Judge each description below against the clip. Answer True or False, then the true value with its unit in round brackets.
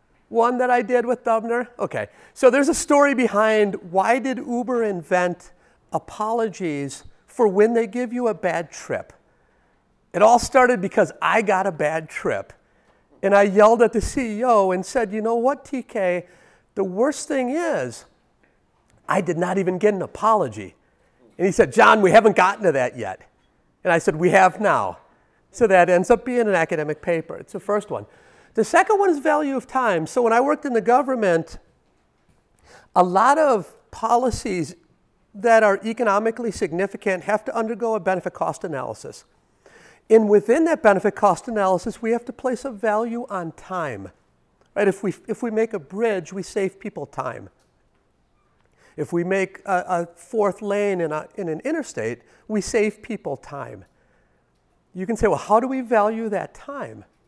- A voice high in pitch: True (210 Hz)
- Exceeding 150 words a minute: True (175 wpm)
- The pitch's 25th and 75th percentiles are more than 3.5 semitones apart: True (4.6 semitones)